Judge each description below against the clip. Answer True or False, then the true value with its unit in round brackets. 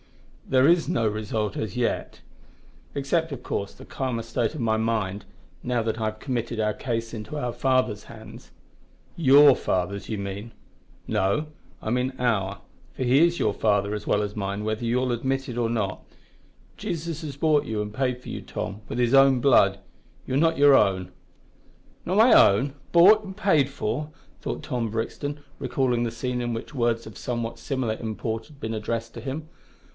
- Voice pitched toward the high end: False (120 Hz)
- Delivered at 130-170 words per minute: False (180 wpm)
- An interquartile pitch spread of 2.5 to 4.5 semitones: True (3.9 semitones)